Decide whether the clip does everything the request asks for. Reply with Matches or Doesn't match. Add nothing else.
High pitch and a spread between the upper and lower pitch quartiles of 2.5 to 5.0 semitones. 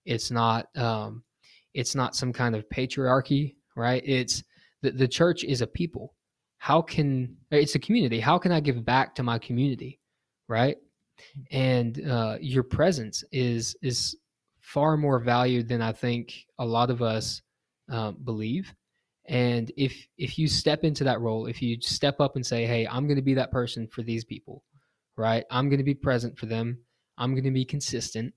Doesn't match